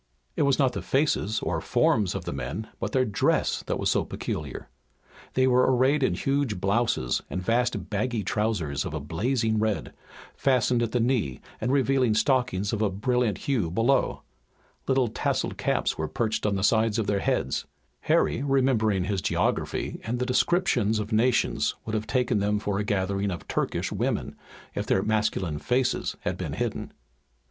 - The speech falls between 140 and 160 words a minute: No, average, 175 wpm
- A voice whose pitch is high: No, low, 110 Hz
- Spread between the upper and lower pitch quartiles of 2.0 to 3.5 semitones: No, average, 4.1 semitones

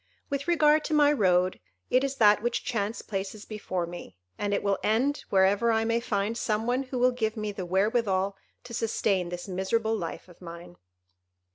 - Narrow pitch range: No, average, 4.0 semitones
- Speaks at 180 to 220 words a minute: Yes, average, 185 wpm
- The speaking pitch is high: Yes, high, 215 Hz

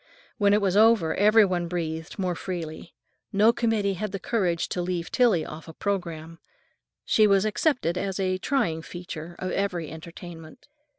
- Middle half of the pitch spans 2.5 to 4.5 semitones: Yes, average, 3.5 semitones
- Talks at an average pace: Yes, average, 165 wpm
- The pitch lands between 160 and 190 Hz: Yes, medium, 185 Hz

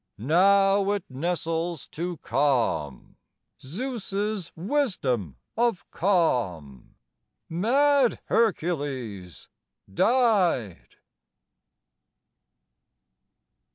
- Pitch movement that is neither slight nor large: No, wide, 8.1 semitones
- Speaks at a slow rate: Yes, slow, 50 wpm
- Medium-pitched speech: Yes, medium, 175 Hz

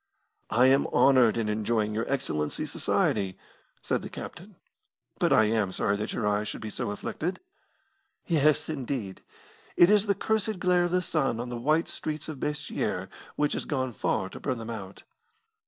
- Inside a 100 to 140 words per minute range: No, average, 175 wpm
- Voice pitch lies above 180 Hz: No, low, 125 Hz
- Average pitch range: No, wide, 6.2 semitones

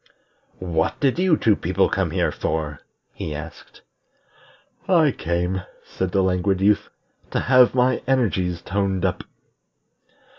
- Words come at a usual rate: No, slow, 125 wpm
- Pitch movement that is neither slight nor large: No, wide, 6.2 semitones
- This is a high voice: No, very low, 95 Hz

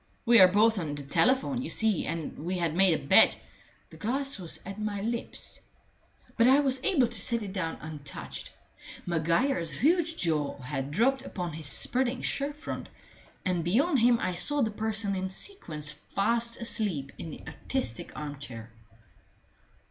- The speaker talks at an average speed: Yes, average, 165 wpm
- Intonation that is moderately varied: No, wide, 7.2 semitones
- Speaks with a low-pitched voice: No, high, 195 Hz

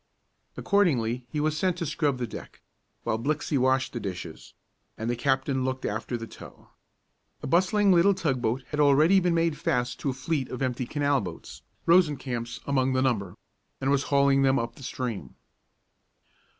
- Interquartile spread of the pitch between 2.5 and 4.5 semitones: Yes, average, 3.9 semitones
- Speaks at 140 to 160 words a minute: No, average, 170 wpm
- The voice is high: No, low, 135 Hz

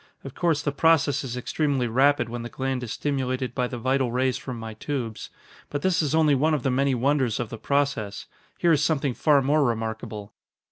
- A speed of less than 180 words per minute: No, fast, 205 wpm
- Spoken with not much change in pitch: No, average, 3.1 semitones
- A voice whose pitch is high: No, low, 135 Hz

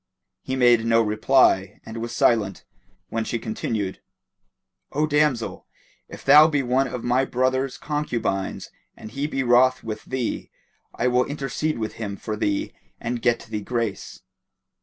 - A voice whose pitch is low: Yes, low, 120 Hz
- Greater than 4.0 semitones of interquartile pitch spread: No, average, 3.0 semitones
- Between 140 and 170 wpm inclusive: Yes, average, 150 wpm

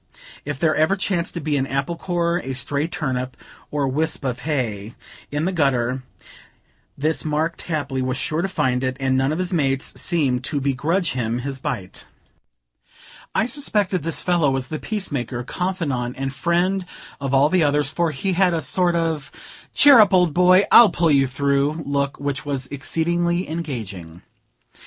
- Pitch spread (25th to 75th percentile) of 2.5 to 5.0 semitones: Yes, average, 4.4 semitones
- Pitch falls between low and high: Yes, medium, 145 Hz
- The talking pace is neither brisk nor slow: Yes, average, 170 wpm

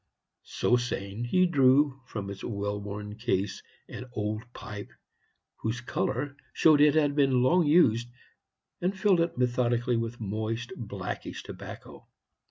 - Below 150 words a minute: Yes, slow, 135 wpm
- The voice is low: Yes, low, 120 Hz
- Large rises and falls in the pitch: No, average, 5.0 semitones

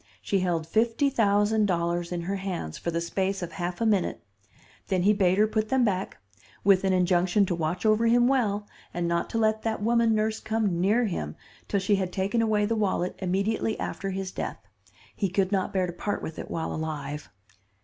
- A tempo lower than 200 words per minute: No, fast, 205 wpm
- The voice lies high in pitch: Yes, high, 195 Hz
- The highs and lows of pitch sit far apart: No, average, 3.5 semitones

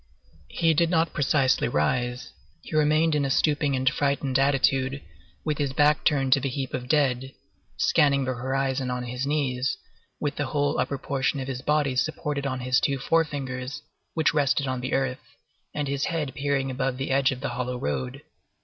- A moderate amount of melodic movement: No, narrow, 2.2 semitones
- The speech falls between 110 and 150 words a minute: No, average, 185 wpm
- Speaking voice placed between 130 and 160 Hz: Yes, low, 135 Hz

